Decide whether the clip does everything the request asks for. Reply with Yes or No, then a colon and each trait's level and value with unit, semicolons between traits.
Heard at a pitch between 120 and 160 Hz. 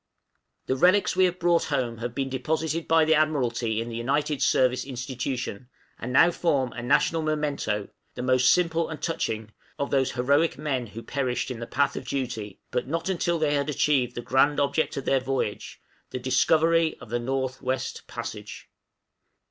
Yes: low, 135 Hz